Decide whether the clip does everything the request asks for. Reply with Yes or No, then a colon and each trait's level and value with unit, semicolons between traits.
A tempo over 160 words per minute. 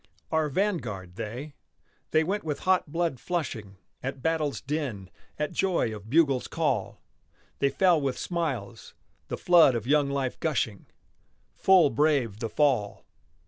No: average, 140 wpm